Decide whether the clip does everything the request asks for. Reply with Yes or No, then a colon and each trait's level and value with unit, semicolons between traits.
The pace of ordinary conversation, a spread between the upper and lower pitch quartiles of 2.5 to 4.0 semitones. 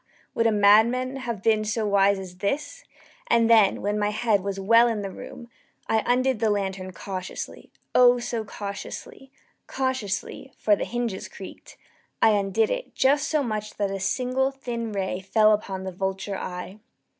Yes: average, 170 wpm; average, 3.7 semitones